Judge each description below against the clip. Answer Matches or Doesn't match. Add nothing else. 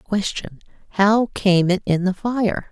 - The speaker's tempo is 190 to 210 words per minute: Doesn't match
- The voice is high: Matches